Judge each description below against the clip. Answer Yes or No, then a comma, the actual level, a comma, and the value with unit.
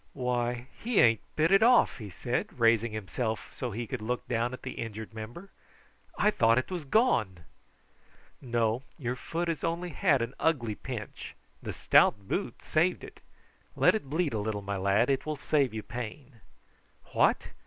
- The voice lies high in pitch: No, low, 120 Hz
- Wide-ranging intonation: Yes, wide, 5.7 semitones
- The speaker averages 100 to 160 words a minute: No, average, 175 wpm